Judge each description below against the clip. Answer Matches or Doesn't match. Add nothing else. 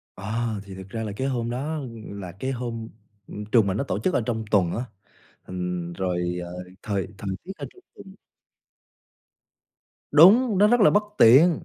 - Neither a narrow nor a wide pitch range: Doesn't match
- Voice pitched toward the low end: Matches